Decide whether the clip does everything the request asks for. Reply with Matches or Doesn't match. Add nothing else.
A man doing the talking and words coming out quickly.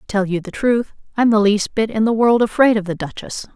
Doesn't match